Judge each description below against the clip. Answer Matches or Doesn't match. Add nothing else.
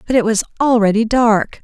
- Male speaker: Doesn't match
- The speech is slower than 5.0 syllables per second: Doesn't match